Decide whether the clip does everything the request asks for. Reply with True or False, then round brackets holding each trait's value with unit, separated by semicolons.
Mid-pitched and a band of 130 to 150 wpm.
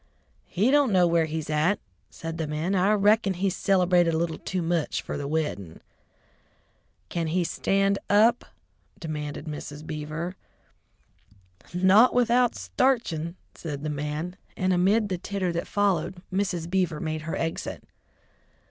True (175 Hz; 140 wpm)